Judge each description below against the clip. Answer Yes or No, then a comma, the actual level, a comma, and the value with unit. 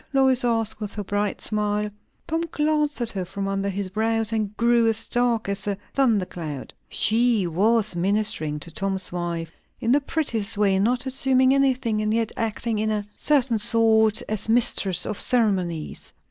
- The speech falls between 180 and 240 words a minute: No, average, 165 wpm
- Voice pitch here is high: Yes, high, 215 Hz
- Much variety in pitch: No, average, 3.3 semitones